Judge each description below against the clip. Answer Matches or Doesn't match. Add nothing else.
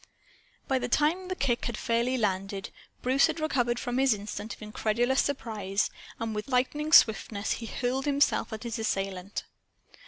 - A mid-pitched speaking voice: Doesn't match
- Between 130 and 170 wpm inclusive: Matches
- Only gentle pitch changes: Doesn't match